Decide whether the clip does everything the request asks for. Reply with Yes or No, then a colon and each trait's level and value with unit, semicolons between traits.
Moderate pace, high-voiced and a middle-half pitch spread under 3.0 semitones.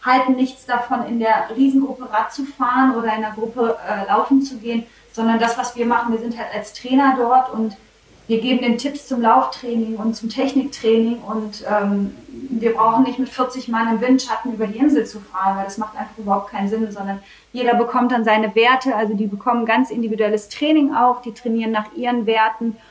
No: fast, 205 wpm; high, 230 Hz; narrow, 2.6 semitones